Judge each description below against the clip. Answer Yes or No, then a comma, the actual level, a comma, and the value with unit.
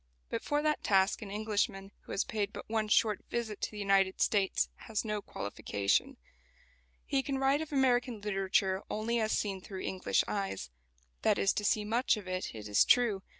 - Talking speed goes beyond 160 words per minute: Yes, average, 190 wpm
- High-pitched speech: Yes, high, 210 Hz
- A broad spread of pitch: No, average, 3.1 semitones